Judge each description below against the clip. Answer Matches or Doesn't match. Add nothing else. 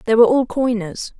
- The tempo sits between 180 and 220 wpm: Matches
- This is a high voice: Matches